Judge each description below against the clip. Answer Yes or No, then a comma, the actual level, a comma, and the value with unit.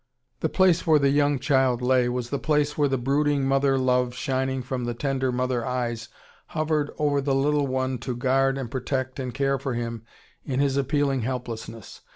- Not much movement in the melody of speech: Yes, narrow, 2.0 semitones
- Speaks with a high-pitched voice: No, low, 135 Hz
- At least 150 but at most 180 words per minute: No, average, 190 wpm